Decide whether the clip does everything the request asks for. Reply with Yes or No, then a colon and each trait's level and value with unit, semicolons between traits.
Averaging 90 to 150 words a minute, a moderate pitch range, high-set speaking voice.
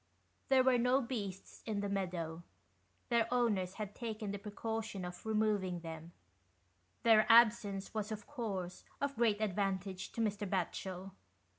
Yes: average, 145 wpm; average, 3.1 semitones; high, 205 Hz